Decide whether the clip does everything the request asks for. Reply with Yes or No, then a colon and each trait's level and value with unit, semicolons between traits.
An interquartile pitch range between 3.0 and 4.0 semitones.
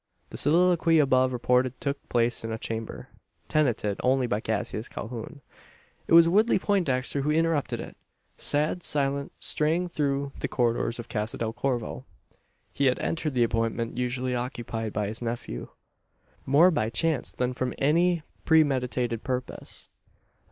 No: average, 4.4 semitones